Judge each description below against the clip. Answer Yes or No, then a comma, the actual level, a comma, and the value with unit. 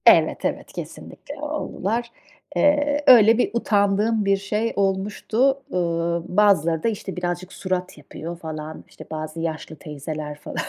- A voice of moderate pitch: No, high, 195 Hz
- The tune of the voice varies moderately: No, wide, 5.8 semitones